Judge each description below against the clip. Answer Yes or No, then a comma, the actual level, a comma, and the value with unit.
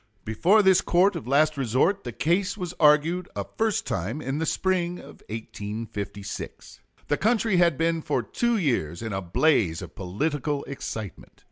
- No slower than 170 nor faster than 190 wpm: No, average, 160 wpm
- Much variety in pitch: Yes, wide, 8.2 semitones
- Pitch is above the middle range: No, medium, 150 Hz